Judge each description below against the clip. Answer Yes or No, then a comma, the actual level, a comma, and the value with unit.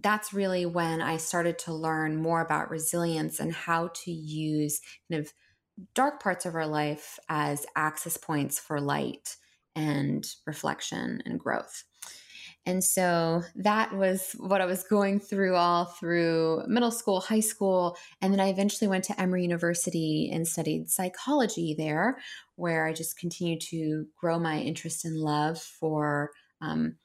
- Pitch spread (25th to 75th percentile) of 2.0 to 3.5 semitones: Yes, average, 3.1 semitones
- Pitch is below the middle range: No, medium, 170 Hz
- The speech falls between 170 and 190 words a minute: No, average, 155 wpm